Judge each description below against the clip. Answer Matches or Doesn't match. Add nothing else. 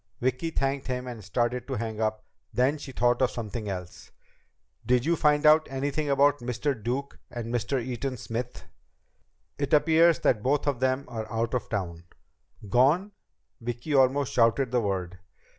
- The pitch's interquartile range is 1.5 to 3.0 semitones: Doesn't match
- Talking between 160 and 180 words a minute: Matches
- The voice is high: Doesn't match